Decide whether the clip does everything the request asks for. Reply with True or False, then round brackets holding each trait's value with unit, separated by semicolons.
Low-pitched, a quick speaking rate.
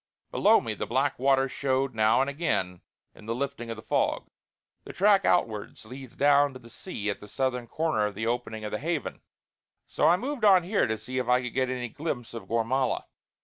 True (130 Hz; 215 wpm)